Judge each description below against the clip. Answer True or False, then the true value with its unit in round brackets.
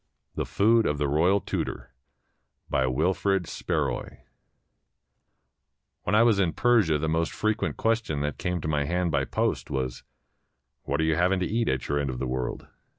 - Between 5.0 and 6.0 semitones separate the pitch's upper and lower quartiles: True (5.6 semitones)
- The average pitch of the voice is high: False (80 Hz)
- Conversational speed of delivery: True (180 wpm)